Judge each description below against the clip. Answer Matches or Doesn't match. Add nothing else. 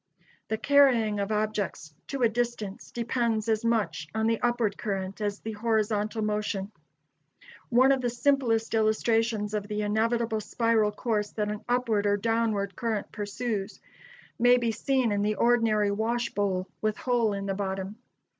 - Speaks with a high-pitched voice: Matches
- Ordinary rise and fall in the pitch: Doesn't match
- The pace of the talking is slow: Doesn't match